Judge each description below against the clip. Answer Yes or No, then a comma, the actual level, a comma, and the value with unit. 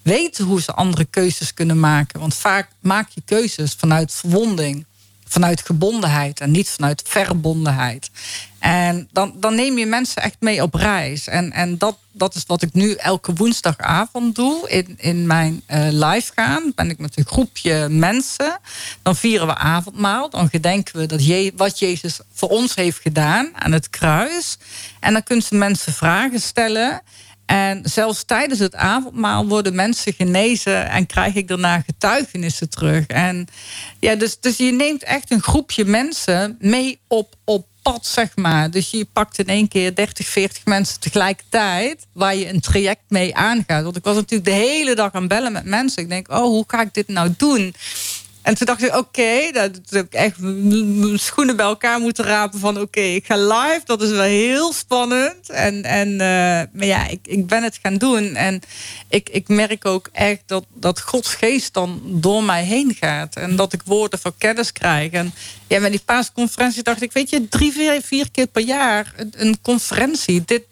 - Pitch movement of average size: Yes, average, 4.7 semitones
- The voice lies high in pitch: Yes, high, 200 Hz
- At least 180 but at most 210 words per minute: Yes, average, 190 wpm